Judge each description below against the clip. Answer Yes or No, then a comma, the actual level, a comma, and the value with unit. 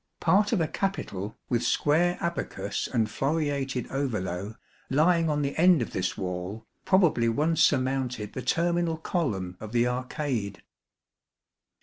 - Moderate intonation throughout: No, wide, 6.8 semitones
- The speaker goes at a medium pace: No, slow, 130 wpm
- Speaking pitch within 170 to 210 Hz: No, low, 135 Hz